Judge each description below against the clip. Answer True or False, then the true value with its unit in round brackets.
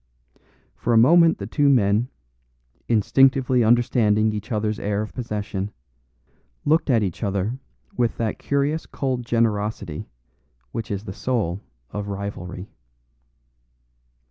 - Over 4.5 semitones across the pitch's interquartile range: False (3.5 semitones)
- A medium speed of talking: False (115 wpm)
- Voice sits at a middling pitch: False (110 Hz)